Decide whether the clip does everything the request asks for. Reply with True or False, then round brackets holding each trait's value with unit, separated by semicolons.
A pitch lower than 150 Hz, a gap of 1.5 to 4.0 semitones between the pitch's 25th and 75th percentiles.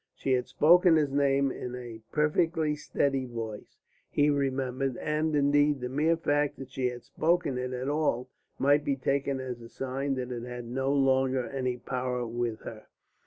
True (135 Hz; 2.6 semitones)